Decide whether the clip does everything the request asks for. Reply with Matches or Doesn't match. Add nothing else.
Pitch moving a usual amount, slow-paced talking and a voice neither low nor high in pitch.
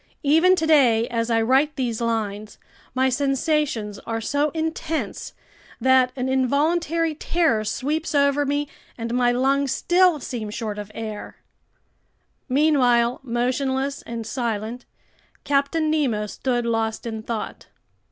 Doesn't match